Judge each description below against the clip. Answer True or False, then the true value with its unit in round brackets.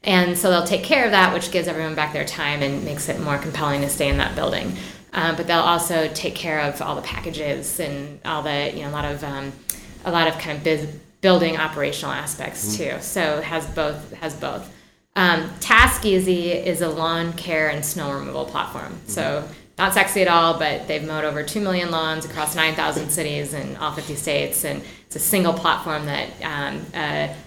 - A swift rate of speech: True (210 wpm)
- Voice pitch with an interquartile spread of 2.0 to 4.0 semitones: True (2.6 semitones)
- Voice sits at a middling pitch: True (155 Hz)